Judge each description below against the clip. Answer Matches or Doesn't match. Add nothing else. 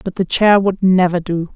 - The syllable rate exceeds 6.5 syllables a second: Doesn't match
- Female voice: Matches